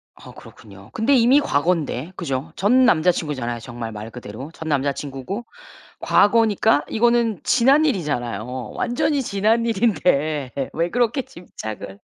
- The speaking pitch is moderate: Yes, medium, 165 Hz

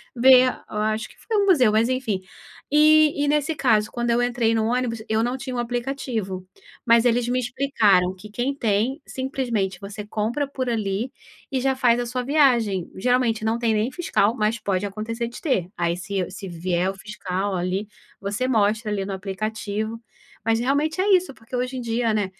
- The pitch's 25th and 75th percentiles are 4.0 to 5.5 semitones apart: No, average, 3.6 semitones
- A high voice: Yes, high, 230 Hz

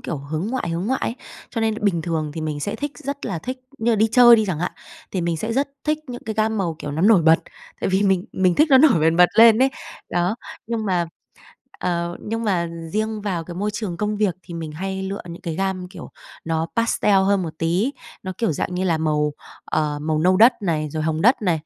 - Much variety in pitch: No, average, 5.0 semitones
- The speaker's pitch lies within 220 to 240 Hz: No, medium, 185 Hz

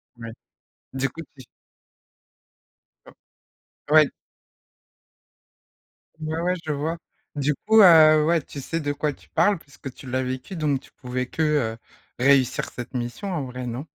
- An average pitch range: Yes, average, 3.6 semitones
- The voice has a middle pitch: Yes, medium, 145 Hz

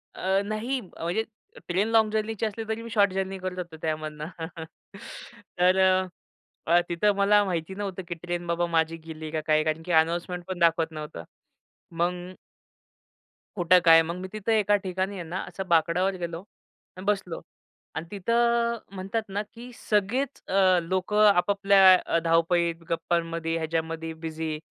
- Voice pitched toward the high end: No, medium, 180 Hz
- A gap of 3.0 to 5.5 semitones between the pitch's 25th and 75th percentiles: Yes, average, 3.3 semitones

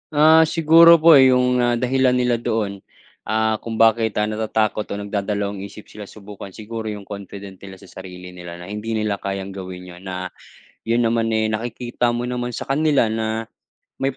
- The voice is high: No, low, 110 Hz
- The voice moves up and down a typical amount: Yes, average, 3.5 semitones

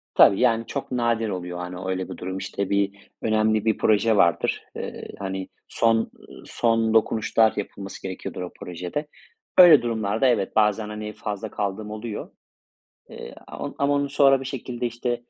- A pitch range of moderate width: Yes, average, 3.0 semitones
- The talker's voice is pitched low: Yes, low, 110 Hz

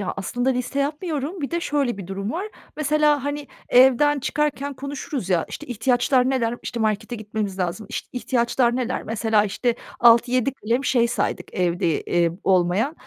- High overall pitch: Yes, high, 245 Hz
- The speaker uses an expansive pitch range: No, average, 4.8 semitones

